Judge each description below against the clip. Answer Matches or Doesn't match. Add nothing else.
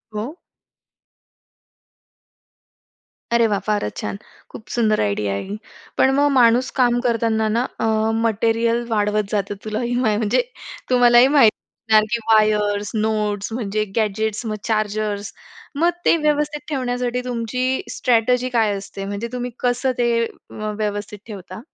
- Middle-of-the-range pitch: Doesn't match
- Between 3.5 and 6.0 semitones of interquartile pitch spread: Doesn't match